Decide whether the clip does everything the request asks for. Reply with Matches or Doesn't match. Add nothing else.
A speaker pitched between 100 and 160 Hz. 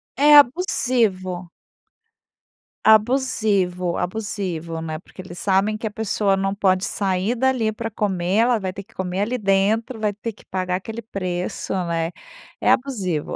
Doesn't match